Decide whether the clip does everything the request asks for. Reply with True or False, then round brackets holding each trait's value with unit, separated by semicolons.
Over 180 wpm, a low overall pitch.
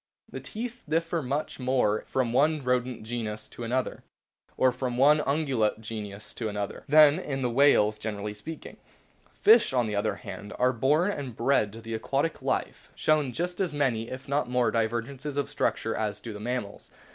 True (190 wpm; 125 Hz)